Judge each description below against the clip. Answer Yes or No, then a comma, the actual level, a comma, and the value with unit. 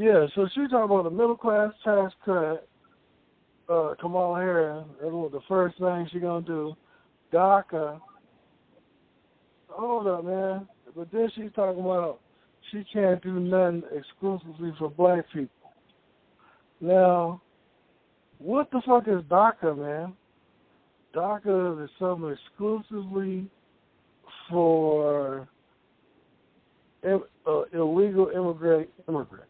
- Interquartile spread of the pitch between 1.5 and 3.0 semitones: No, average, 3.5 semitones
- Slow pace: Yes, slow, 110 wpm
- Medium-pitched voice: Yes, medium, 180 Hz